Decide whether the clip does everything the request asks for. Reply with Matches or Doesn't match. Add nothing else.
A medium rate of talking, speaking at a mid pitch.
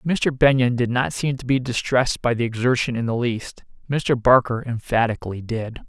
Doesn't match